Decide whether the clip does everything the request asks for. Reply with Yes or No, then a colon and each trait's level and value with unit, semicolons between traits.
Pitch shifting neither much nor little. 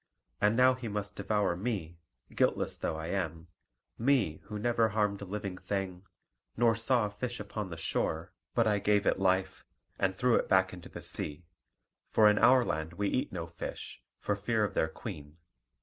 Yes: average, 3.9 semitones